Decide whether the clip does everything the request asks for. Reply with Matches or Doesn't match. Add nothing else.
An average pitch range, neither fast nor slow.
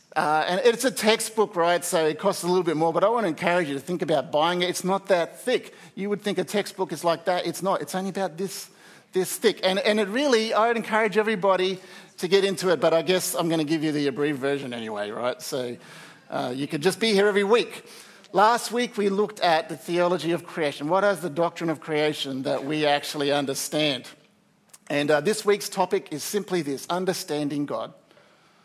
Doesn't match